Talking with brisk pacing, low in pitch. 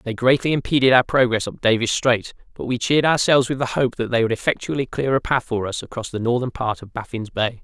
Yes: fast, 245 wpm; low, 120 Hz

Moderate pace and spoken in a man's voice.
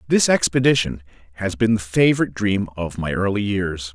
Yes: average, 165 wpm; male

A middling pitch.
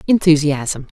Yes: medium, 155 Hz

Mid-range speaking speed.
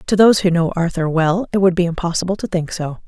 No: fast, 255 wpm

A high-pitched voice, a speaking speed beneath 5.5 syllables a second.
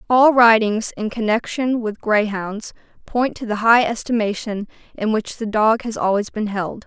Yes: high, 220 Hz; 4.5 syllables/s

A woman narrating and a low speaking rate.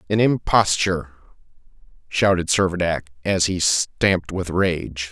No: male; slow, 105 wpm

